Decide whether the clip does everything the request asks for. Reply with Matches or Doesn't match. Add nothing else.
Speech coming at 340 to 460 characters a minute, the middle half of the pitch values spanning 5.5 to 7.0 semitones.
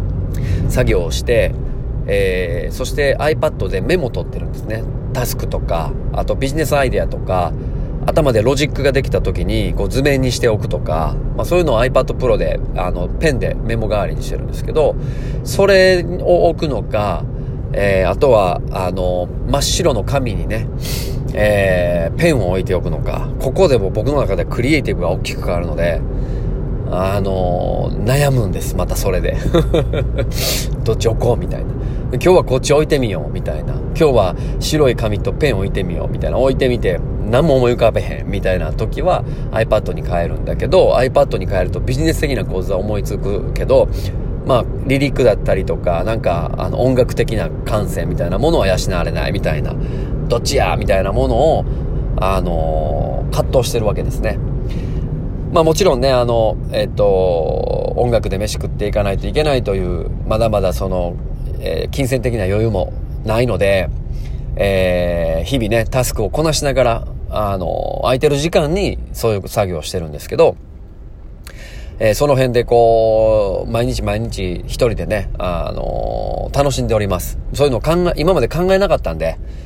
Matches